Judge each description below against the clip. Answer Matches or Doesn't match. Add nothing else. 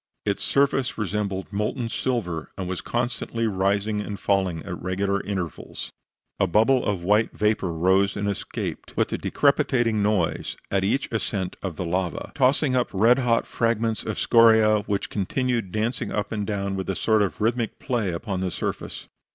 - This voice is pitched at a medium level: Doesn't match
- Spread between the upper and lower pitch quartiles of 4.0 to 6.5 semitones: Doesn't match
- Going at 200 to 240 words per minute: Doesn't match